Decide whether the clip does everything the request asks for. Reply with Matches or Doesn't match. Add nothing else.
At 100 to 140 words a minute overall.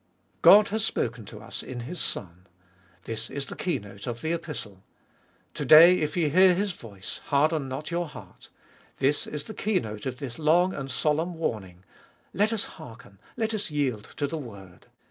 Doesn't match